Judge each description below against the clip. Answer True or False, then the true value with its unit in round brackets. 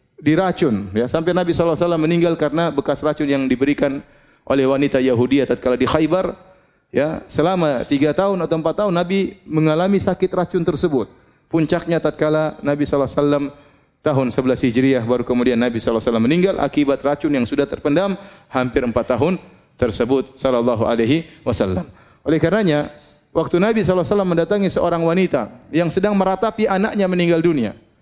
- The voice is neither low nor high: True (155 Hz)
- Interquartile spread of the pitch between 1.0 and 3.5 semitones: False (4.6 semitones)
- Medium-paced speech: False (145 wpm)